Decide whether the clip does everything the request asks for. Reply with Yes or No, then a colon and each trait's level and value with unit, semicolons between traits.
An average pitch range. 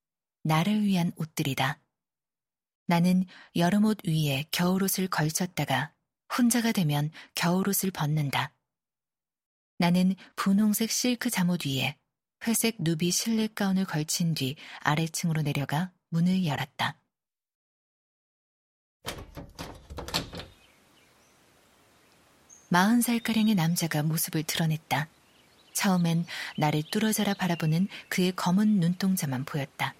Yes: average, 4.3 semitones